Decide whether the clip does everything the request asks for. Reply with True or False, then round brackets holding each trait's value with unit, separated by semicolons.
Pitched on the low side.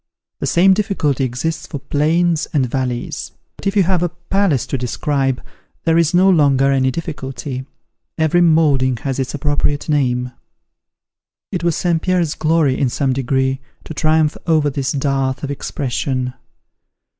False (145 Hz)